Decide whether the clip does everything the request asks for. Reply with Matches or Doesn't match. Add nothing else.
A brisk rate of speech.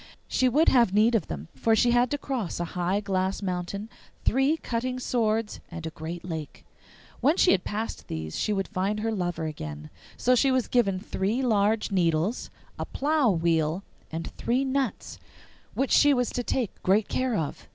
Doesn't match